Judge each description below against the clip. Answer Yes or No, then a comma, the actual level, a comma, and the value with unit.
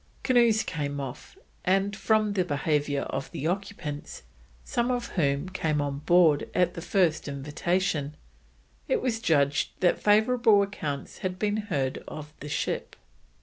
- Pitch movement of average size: No, wide, 6.1 semitones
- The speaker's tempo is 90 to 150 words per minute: Yes, average, 145 wpm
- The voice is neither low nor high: Yes, medium, 175 Hz